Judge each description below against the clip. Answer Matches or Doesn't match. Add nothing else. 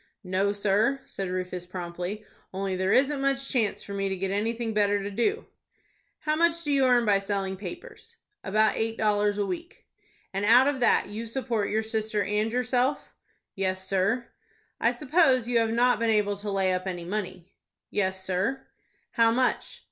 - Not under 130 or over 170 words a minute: Doesn't match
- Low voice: Doesn't match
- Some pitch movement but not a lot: Matches